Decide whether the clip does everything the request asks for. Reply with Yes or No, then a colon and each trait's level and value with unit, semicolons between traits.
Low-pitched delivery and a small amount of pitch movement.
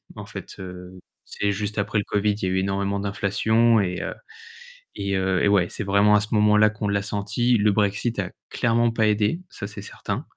Yes: low, 105 Hz; narrow, 1.4 semitones